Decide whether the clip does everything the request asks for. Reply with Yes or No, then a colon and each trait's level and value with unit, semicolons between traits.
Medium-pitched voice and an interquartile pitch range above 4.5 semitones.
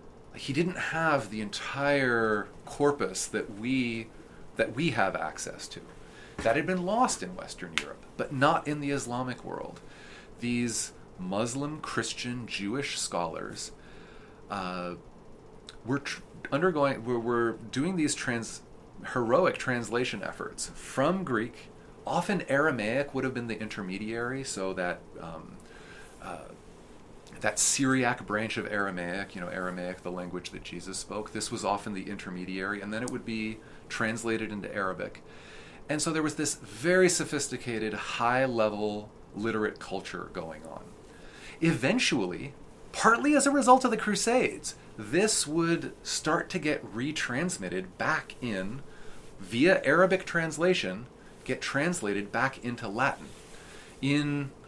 No: low, 120 Hz; wide, 5.4 semitones